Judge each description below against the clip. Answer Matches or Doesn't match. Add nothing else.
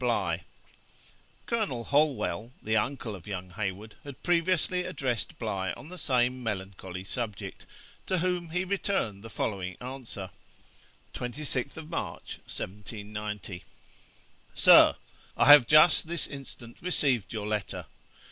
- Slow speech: Matches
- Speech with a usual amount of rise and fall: Doesn't match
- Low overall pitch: Matches